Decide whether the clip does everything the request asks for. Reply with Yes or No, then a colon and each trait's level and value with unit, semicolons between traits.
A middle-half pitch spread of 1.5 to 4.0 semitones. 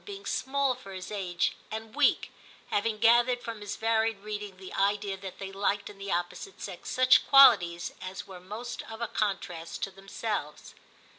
Yes: average, 2.9 semitones